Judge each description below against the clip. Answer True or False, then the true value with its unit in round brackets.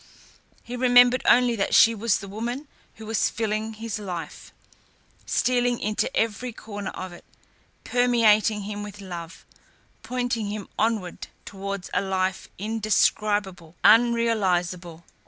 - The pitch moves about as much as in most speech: True (3.0 semitones)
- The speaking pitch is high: True (215 Hz)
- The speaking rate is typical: False (120 wpm)